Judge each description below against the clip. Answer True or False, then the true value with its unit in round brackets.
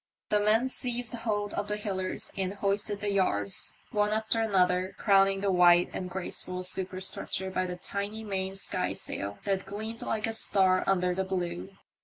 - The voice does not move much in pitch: True (2.1 semitones)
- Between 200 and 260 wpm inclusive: False (165 wpm)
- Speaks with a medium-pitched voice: False (195 Hz)